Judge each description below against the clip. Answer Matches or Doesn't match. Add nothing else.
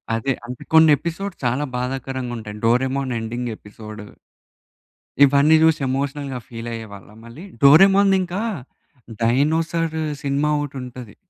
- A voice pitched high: Doesn't match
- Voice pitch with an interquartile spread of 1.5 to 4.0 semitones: Doesn't match